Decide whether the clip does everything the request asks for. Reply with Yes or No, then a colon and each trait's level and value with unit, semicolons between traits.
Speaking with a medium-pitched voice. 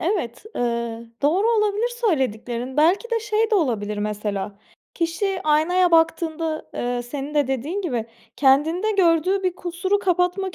No: very high, 325 Hz